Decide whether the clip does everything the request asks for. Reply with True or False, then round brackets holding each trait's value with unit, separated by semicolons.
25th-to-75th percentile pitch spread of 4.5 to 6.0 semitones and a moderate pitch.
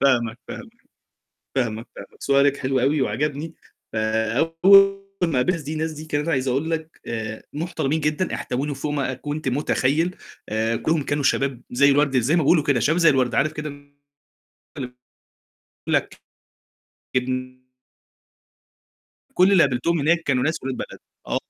False (3.7 semitones; 145 Hz)